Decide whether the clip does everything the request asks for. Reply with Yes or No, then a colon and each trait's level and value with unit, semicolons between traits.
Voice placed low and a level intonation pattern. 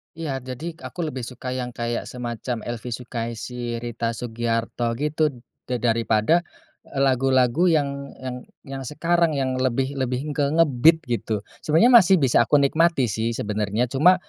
No: low, 130 Hz; average, 3.9 semitones